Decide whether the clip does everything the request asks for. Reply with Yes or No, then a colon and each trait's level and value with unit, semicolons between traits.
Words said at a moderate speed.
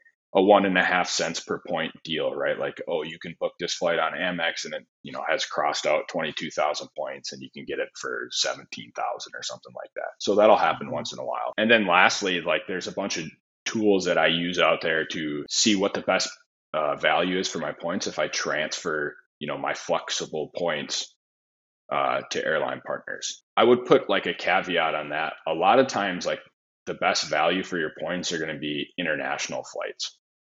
No: fast, 210 wpm